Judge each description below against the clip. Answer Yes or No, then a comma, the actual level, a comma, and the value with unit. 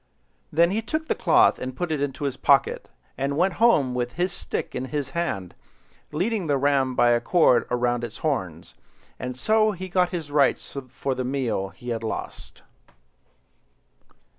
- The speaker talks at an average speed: Yes, average, 170 wpm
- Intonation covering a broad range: Yes, wide, 6.0 semitones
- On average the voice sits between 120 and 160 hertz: Yes, medium, 140 Hz